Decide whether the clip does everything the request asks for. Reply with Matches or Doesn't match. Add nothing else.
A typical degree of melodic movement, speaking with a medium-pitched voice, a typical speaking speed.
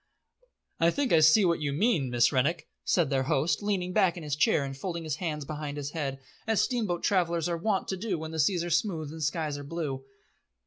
Doesn't match